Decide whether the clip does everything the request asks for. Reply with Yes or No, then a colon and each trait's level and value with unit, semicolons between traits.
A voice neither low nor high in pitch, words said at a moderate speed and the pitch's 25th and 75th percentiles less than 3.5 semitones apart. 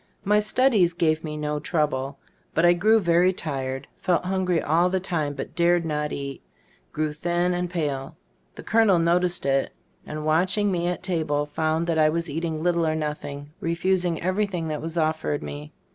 Yes: medium, 165 Hz; average, 175 wpm; average, 2.8 semitones